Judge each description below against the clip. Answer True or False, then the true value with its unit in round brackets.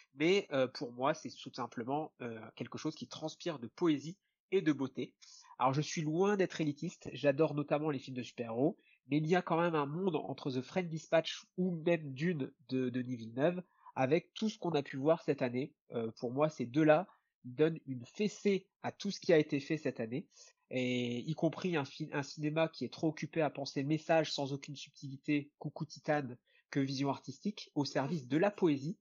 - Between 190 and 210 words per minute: True (195 wpm)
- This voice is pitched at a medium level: True (150 Hz)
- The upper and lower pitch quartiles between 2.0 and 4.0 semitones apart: True (3.7 semitones)